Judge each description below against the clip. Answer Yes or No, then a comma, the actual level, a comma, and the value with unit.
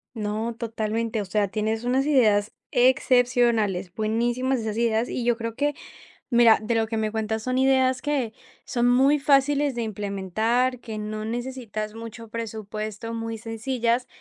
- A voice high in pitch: Yes, high, 230 Hz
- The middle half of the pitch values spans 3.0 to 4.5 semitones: No, narrow, 2.5 semitones